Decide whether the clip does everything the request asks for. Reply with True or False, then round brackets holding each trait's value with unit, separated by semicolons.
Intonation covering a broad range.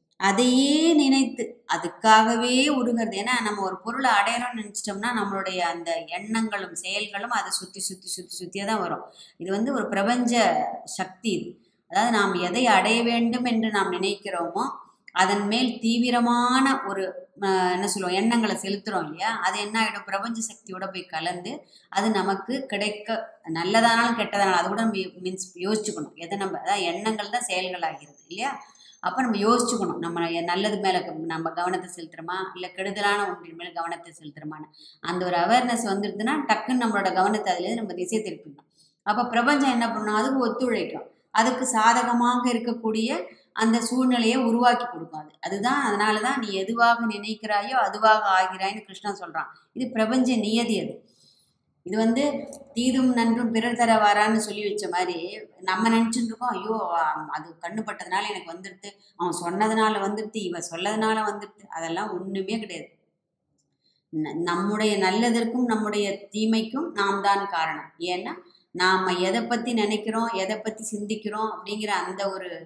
False (3.9 semitones)